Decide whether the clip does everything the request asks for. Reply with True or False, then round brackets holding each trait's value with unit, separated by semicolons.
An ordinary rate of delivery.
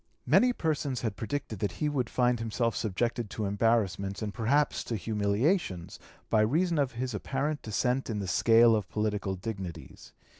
True (160 wpm)